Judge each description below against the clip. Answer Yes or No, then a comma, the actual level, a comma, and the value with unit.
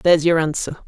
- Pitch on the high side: No, medium, 160 Hz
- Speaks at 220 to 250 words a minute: No, fast, 205 wpm